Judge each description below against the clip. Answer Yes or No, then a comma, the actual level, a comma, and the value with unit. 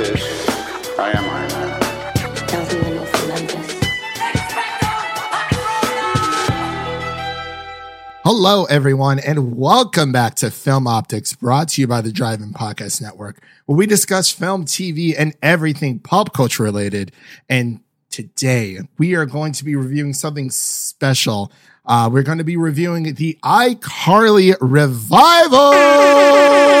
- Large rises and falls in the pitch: Yes, wide, 5.9 semitones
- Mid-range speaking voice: Yes, medium, 145 Hz